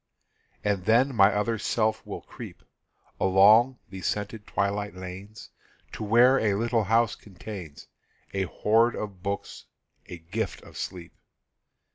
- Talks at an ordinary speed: No, slow, 130 wpm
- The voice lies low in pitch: Yes, low, 105 Hz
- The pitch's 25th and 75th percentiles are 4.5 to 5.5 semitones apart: No, average, 2.7 semitones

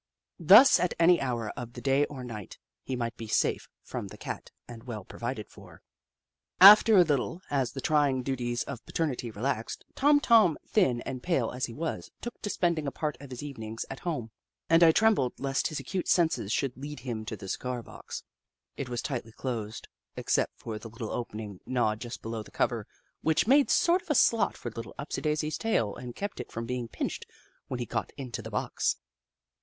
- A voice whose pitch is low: Yes, low, 130 Hz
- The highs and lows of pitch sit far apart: Yes, wide, 5.7 semitones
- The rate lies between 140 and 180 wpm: No, average, 200 wpm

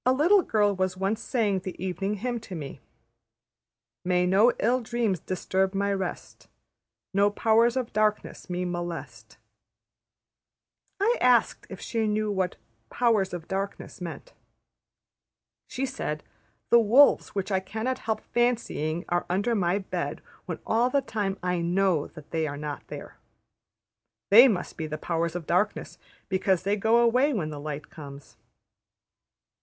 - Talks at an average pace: Yes, average, 145 wpm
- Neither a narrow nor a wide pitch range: Yes, average, 4.5 semitones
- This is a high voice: Yes, high, 195 Hz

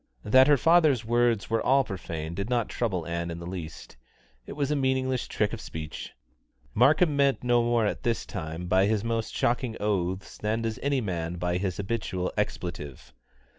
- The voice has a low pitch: Yes, low, 110 Hz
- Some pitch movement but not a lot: No, wide, 5.8 semitones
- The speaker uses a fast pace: No, average, 180 wpm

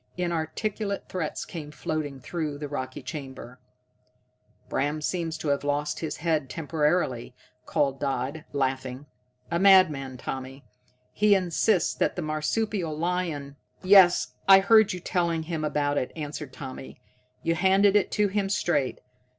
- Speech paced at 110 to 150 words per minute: Yes, average, 140 wpm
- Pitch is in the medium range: Yes, medium, 155 Hz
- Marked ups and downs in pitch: No, average, 4.4 semitones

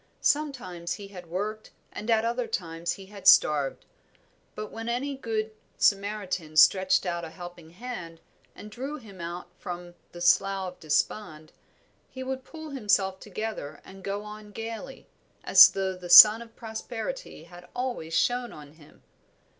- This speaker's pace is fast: No, average, 155 wpm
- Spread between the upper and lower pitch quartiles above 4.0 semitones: Yes, average, 4.6 semitones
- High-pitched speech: Yes, high, 200 Hz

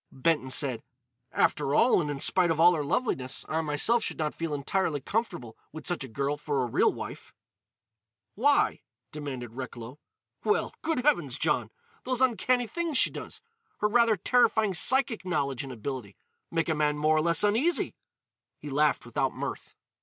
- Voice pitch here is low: No, medium, 155 Hz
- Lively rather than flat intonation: Yes, wide, 8.5 semitones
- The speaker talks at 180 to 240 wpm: No, average, 155 wpm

